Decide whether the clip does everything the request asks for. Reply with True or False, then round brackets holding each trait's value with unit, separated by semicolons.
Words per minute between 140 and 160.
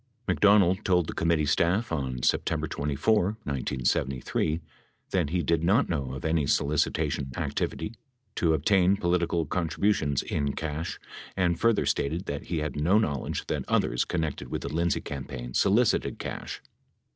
True (145 wpm)